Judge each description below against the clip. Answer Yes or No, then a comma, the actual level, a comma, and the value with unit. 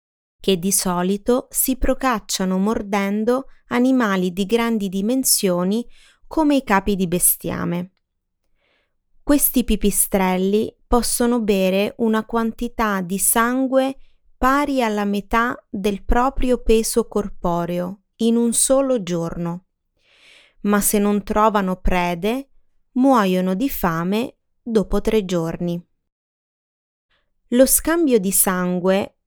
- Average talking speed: No, slow, 100 wpm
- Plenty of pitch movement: No, average, 4.2 semitones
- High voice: Yes, high, 215 Hz